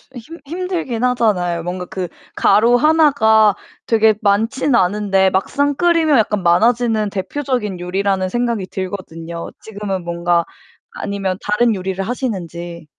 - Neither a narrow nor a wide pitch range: Yes, average, 4.6 semitones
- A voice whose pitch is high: Yes, high, 210 Hz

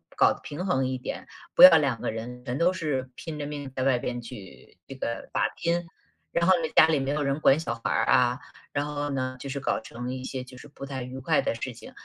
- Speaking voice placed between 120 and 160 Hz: Yes, low, 135 Hz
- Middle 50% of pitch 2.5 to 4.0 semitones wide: Yes, average, 2.9 semitones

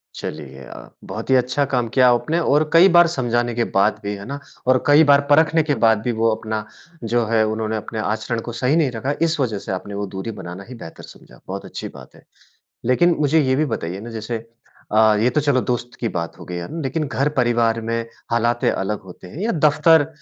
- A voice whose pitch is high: No, low, 120 Hz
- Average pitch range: Yes, average, 4.7 semitones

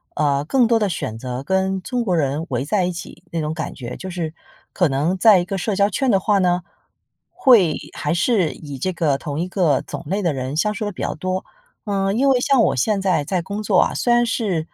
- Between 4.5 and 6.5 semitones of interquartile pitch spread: Yes, average, 5.1 semitones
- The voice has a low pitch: No, medium, 185 Hz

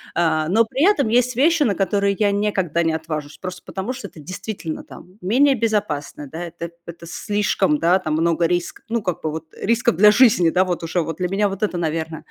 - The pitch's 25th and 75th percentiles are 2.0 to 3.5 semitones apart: No, average, 4.4 semitones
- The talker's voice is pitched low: No, medium, 185 Hz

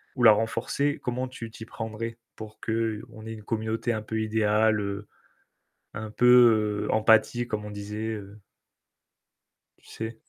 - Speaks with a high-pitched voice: No, low, 110 Hz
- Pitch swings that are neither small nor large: No, narrow, 1.2 semitones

